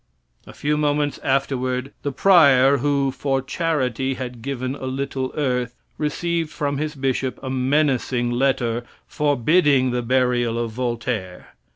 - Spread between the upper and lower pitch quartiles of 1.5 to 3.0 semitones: Yes, narrow, 2.5 semitones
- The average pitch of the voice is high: No, low, 135 Hz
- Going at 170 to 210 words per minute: No, slow, 135 wpm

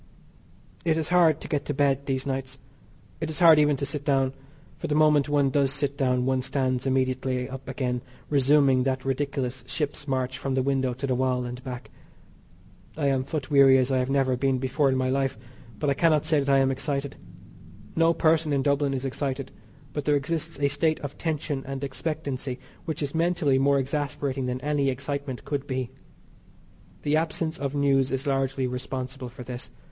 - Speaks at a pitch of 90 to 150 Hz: Yes, low, 135 Hz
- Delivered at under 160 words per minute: No, average, 195 wpm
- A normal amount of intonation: No, narrow, 1.9 semitones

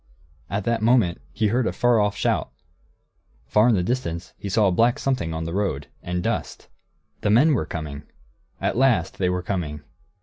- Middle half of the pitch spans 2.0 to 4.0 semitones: No, wide, 5.5 semitones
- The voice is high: No, low, 100 Hz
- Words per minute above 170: Yes, average, 190 wpm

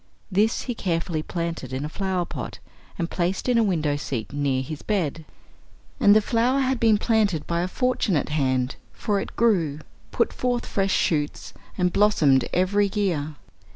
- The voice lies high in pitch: No, medium, 180 Hz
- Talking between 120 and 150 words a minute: No, average, 165 wpm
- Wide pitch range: Yes, wide, 5.8 semitones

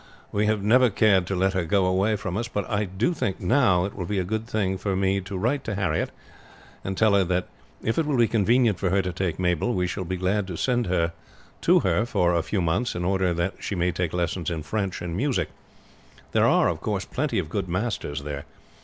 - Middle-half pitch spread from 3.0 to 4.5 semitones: Yes, average, 3.3 semitones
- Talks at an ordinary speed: No, fast, 240 wpm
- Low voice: Yes, very low, 95 Hz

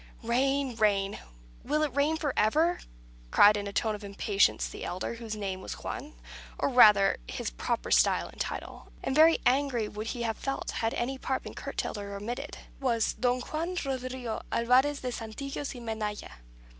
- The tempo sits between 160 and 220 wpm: Yes, average, 175 wpm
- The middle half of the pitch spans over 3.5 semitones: Yes, average, 4.5 semitones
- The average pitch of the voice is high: Yes, high, 240 Hz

